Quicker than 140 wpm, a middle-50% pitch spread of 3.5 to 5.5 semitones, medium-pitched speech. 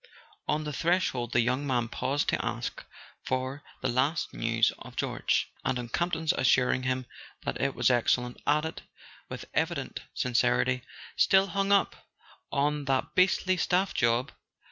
No: average, 150 wpm; average, 4.5 semitones; low, 130 Hz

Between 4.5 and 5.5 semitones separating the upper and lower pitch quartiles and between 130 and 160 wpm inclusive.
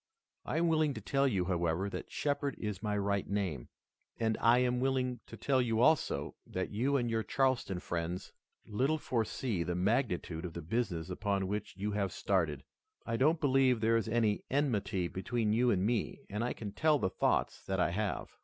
No: average, 5.0 semitones; average, 190 wpm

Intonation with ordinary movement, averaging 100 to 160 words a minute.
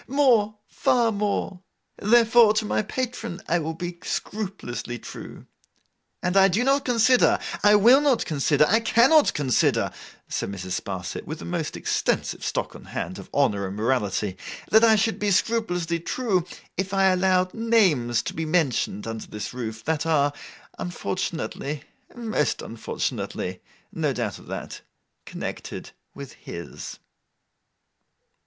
No: wide, 8.1 semitones; slow, 135 wpm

